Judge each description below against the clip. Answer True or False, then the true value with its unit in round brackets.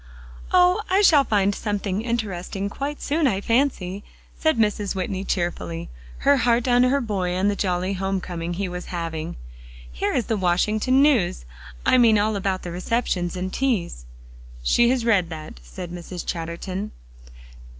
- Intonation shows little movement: False (5.0 semitones)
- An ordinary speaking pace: True (160 wpm)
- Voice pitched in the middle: False (200 Hz)